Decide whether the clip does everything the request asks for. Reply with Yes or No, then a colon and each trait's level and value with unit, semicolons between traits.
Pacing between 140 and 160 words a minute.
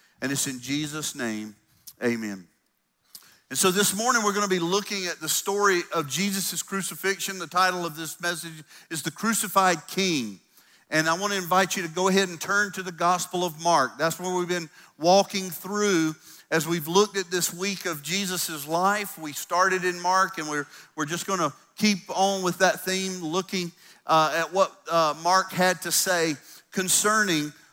No: average, 185 wpm